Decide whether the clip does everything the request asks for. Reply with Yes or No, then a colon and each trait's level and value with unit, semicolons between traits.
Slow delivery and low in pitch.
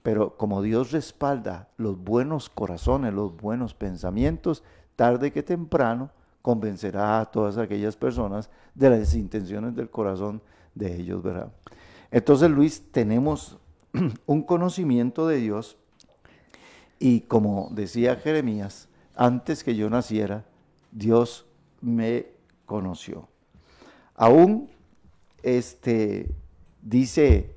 Yes: slow, 100 wpm; low, 115 Hz